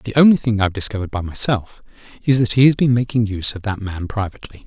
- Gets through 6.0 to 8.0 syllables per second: Yes, 6.8 syllables/s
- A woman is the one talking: No, male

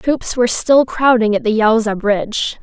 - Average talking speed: Yes, average, 185 wpm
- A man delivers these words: No, female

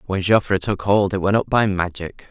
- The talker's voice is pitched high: No, very low, 95 Hz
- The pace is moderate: No, fast, 235 wpm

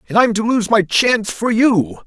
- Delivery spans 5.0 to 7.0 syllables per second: No, 4.8 syllables/s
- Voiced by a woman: No, male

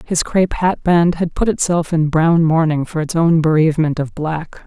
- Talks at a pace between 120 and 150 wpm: No, fast, 205 wpm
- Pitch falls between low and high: Yes, medium, 165 Hz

